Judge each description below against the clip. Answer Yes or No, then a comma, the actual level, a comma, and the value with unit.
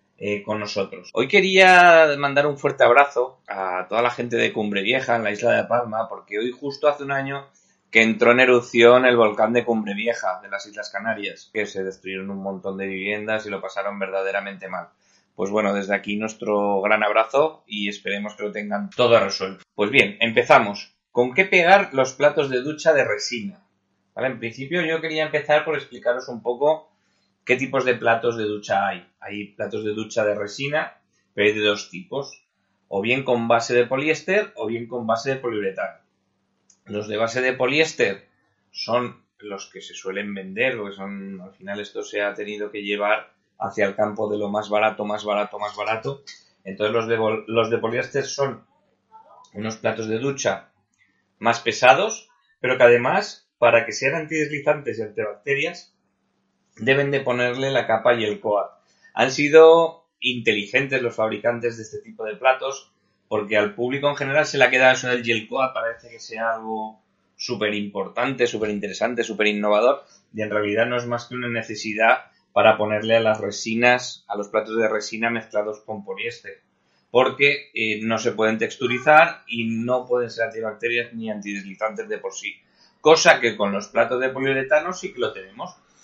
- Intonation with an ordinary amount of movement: Yes, average, 4.2 semitones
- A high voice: No, low, 115 Hz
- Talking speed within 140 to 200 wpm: Yes, average, 185 wpm